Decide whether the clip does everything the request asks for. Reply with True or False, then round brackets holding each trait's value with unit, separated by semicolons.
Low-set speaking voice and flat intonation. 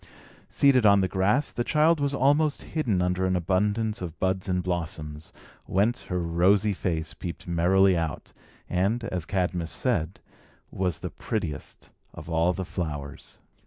False (95 Hz; 3.6 semitones)